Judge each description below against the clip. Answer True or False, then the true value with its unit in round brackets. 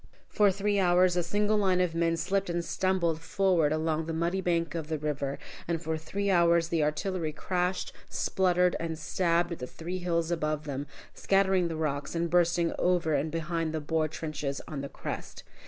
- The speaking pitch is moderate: True (170 Hz)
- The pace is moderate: True (190 wpm)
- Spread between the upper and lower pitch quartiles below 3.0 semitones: True (2.4 semitones)